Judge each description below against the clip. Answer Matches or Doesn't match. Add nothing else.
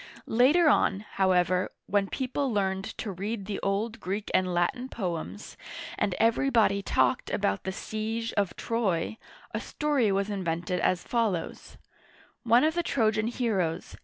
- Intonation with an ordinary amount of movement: Matches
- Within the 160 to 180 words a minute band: Doesn't match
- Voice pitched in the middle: Doesn't match